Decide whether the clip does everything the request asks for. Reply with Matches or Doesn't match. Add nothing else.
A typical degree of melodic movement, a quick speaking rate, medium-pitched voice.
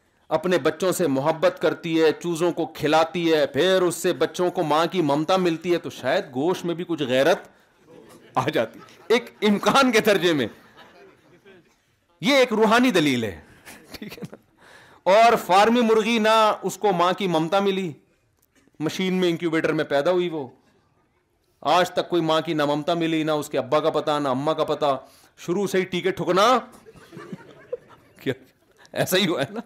Doesn't match